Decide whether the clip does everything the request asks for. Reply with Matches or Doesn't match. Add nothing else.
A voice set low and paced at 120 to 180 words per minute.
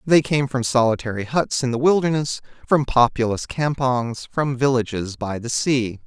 Matches